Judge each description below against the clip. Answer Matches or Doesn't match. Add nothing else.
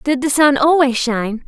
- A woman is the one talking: Matches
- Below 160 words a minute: Doesn't match